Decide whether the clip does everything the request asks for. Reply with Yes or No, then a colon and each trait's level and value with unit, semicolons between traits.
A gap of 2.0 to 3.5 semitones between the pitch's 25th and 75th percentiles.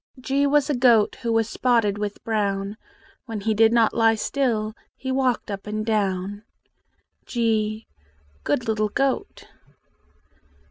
Yes: narrow, 2.6 semitones